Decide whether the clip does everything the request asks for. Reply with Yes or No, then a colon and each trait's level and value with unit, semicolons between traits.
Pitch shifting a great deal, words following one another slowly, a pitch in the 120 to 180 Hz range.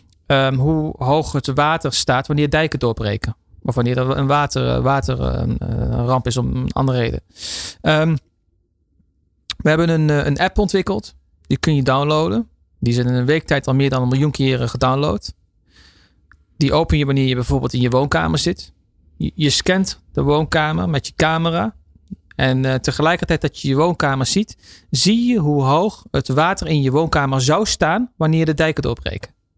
No: wide, 5.9 semitones; average, 170 wpm; low, 135 Hz